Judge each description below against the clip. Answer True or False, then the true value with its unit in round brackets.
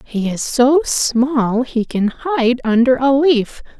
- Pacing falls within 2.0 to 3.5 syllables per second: True (3.2 syllables/s)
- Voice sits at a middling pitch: False (255 Hz)